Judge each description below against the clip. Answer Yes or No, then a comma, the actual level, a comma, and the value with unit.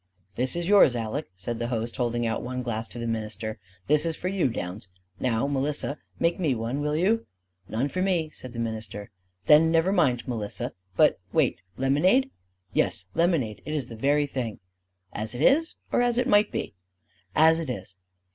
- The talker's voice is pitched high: No, low, 135 Hz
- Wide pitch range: Yes, wide, 6.1 semitones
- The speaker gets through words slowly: No, average, 185 wpm